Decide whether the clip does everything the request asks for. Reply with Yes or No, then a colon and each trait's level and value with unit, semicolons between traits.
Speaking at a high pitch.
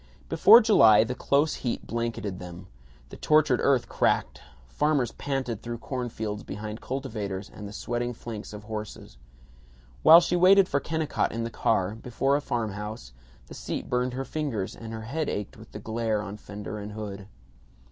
No: low, 115 Hz